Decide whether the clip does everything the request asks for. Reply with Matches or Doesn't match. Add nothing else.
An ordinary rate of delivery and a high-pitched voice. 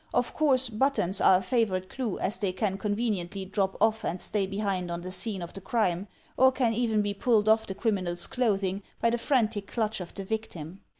Doesn't match